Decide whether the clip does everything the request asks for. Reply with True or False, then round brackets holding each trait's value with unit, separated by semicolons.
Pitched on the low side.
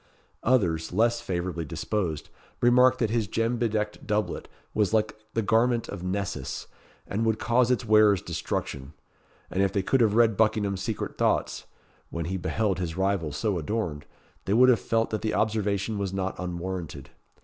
True (105 Hz)